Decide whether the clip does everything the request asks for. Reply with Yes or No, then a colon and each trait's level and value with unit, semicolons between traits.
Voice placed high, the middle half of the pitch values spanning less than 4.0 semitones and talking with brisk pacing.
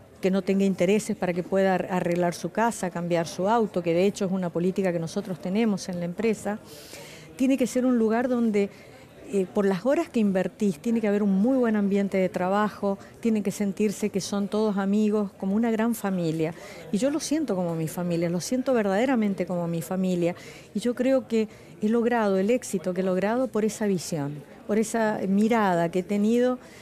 Yes: high, 200 Hz; average, 3.4 semitones; fast, 200 wpm